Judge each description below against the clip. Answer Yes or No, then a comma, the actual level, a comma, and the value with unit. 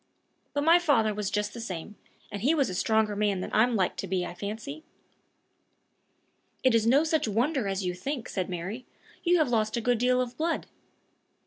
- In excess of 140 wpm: Yes, average, 200 wpm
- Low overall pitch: No, high, 220 Hz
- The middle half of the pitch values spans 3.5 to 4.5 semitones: No, average, 4.9 semitones